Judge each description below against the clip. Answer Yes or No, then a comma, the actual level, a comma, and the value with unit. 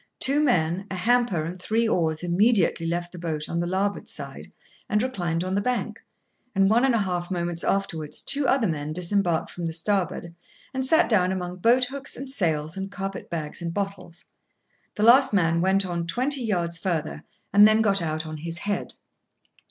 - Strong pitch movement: No, average, 4.3 semitones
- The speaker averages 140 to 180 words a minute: No, average, 190 wpm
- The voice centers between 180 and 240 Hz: Yes, medium, 185 Hz